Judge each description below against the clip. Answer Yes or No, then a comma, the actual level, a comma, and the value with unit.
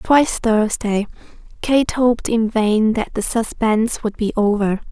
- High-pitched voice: Yes, high, 220 Hz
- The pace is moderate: Yes, average, 145 wpm